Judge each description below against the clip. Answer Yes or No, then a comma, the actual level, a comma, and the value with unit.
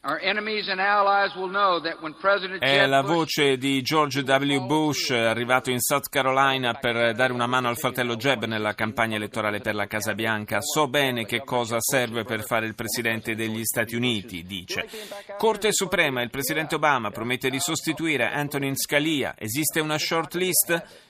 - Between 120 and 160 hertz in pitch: Yes, low, 135 Hz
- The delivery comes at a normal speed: Yes, average, 145 wpm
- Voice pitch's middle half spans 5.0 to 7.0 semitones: Yes, wide, 5.4 semitones